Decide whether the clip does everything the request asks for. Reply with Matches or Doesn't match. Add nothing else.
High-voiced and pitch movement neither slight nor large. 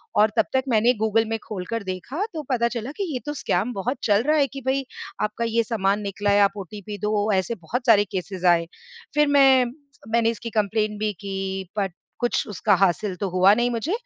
Matches